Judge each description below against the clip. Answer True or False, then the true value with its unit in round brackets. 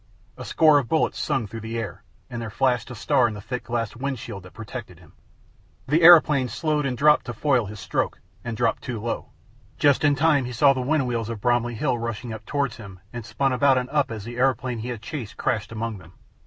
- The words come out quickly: True (235 wpm)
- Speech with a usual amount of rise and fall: True (3.5 semitones)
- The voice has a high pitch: False (120 Hz)